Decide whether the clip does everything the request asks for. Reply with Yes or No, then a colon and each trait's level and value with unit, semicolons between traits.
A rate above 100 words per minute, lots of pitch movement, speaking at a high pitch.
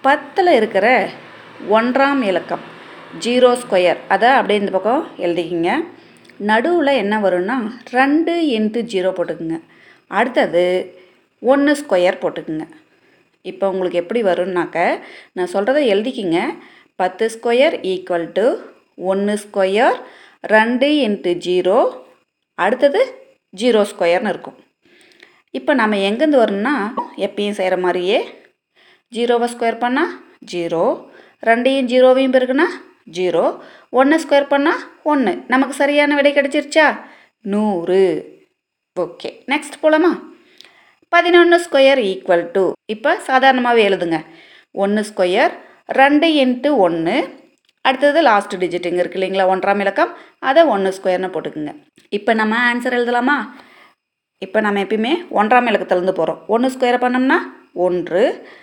Yes: average, 110 wpm; wide, 7.6 semitones; high, 240 Hz